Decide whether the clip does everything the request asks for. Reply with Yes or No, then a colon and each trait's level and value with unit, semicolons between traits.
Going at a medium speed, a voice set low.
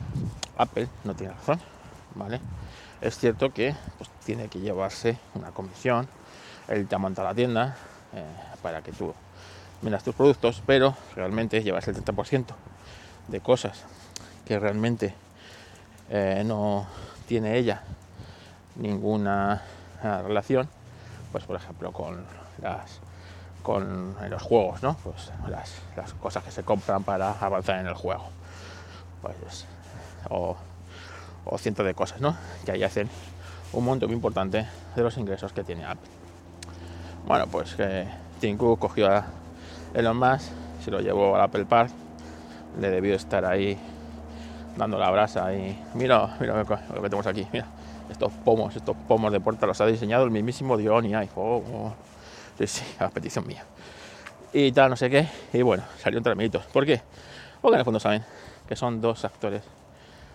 Yes: average, 150 wpm; low, 100 Hz